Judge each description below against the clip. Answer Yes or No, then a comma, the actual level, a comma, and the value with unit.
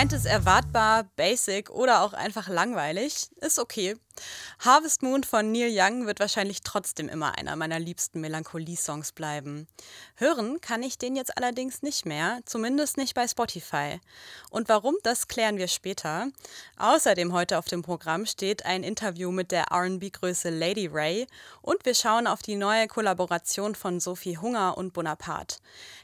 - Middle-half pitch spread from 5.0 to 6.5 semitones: Yes, average, 5.3 semitones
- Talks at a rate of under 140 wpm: No, average, 155 wpm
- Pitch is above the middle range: Yes, high, 200 Hz